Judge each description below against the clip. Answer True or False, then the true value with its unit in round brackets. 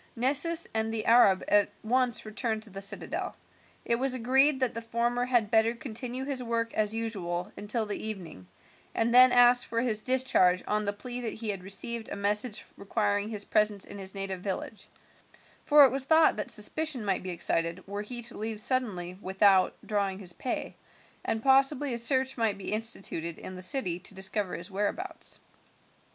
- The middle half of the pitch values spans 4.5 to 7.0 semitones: False (3.7 semitones)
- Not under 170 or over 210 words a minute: True (185 wpm)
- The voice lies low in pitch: False (220 Hz)